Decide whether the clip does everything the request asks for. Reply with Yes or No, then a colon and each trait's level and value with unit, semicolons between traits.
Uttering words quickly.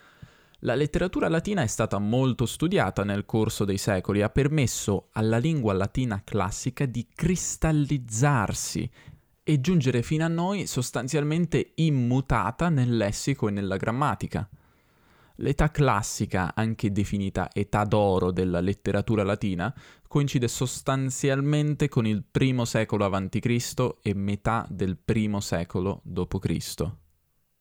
No: slow, 115 wpm